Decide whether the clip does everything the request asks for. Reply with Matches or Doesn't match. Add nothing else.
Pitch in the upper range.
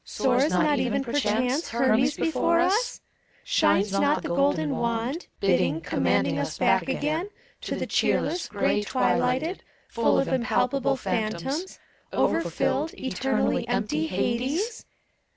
Matches